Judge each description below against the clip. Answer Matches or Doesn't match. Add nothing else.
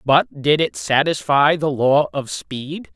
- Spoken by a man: Matches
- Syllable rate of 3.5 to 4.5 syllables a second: Matches